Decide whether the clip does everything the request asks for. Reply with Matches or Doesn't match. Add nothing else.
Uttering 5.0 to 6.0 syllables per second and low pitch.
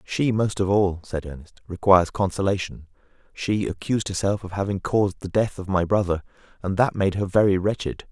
Matches